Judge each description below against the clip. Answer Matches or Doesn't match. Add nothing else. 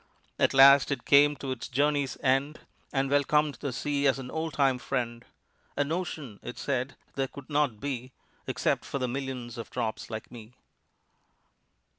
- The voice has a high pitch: Doesn't match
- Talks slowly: Doesn't match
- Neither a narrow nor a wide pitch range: Doesn't match